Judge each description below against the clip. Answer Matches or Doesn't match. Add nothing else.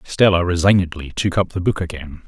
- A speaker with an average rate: Matches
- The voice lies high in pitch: Doesn't match